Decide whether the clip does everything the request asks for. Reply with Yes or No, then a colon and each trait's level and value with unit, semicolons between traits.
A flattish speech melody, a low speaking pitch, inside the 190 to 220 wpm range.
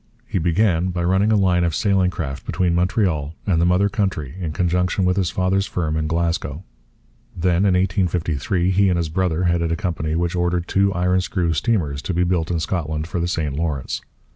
Yes: narrow, 2.2 semitones; very low, 90 Hz; average, 200 wpm